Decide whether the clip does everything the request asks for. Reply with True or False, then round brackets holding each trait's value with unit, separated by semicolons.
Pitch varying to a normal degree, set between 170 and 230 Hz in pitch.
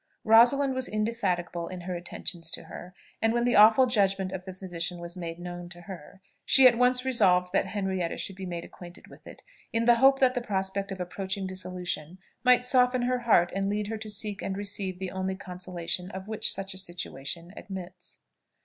True (3.9 semitones; 190 Hz)